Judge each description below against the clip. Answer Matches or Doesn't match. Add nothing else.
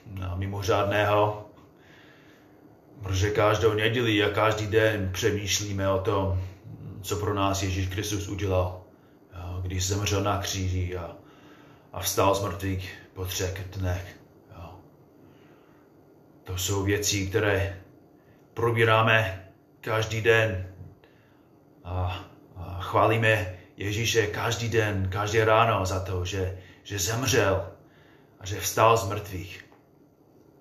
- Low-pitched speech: Matches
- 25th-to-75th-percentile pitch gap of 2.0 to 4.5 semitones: Matches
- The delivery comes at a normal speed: Doesn't match